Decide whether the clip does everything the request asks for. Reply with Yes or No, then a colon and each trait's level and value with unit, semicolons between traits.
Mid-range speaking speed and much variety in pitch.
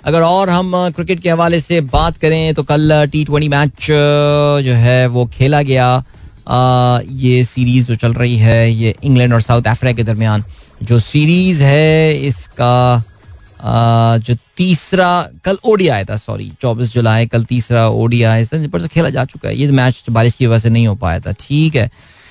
No: average, 180 wpm; average, 4.7 semitones